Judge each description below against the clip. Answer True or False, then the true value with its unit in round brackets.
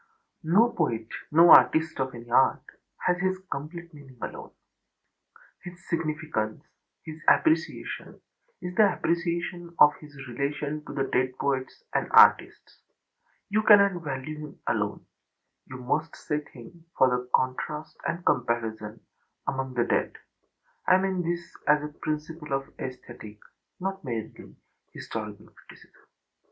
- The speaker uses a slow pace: True (125 wpm)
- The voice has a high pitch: False (150 Hz)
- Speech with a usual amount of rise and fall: True (4.9 semitones)